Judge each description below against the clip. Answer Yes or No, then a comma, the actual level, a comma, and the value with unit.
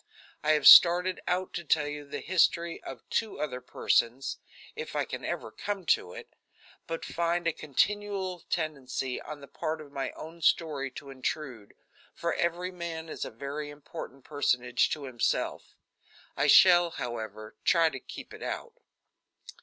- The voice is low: No, medium, 155 Hz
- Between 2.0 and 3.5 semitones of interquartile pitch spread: No, average, 4.1 semitones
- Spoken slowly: No, average, 160 wpm